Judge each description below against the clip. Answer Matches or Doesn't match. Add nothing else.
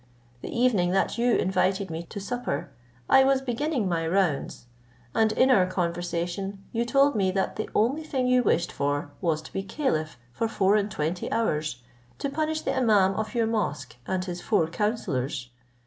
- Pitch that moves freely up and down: Matches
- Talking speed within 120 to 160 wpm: Doesn't match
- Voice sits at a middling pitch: Doesn't match